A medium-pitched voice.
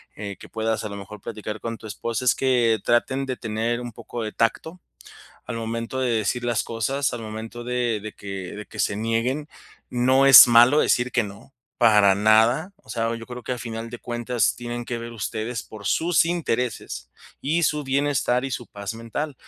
No: low, 115 Hz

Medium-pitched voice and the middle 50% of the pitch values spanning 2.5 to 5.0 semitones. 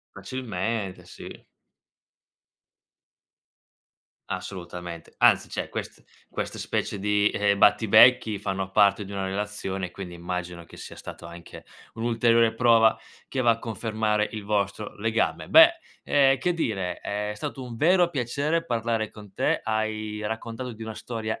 No: low, 110 Hz; average, 2.8 semitones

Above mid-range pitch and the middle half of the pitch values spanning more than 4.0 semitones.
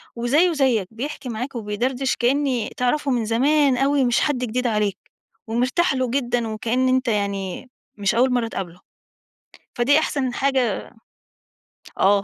No: high, 245 Hz; average, 3.2 semitones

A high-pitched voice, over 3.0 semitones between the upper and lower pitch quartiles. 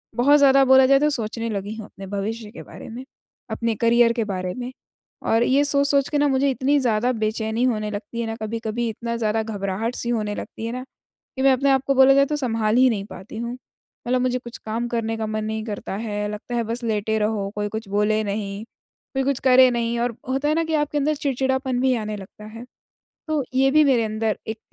Yes: high, 235 Hz; average, 3.4 semitones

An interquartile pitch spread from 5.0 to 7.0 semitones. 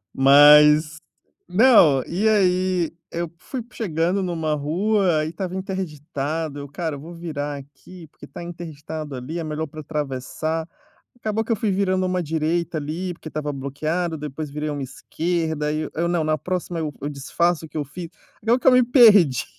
No: average, 3.3 semitones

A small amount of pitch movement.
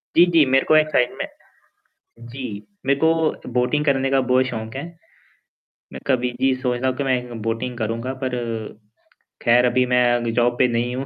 Yes: narrow, 1.8 semitones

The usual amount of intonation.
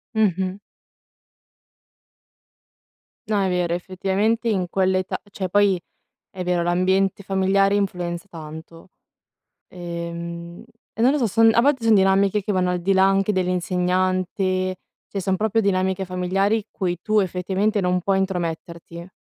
No: narrow, 1.8 semitones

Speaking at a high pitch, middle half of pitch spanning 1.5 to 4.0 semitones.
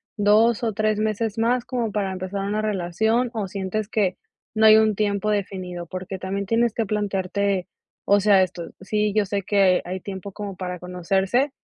Yes: high, 200 Hz; narrow, 2.4 semitones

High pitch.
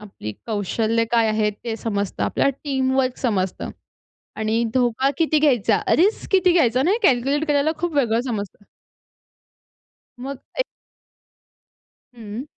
Yes: high, 245 Hz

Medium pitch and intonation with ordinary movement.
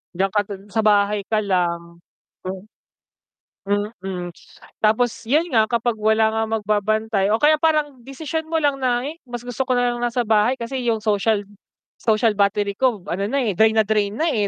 No: high, 220 Hz; average, 3.2 semitones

